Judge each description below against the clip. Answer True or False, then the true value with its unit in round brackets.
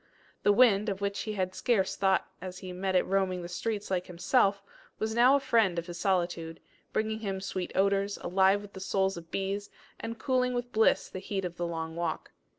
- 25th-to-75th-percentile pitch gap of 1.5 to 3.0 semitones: True (2.6 semitones)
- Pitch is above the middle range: True (195 Hz)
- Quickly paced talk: True (210 wpm)